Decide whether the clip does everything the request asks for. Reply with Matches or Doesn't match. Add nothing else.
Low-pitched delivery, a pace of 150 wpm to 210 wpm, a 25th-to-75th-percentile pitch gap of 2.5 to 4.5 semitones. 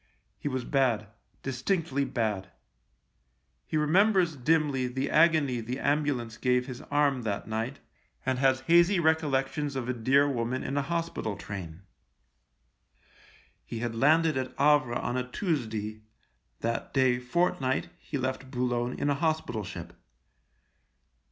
Doesn't match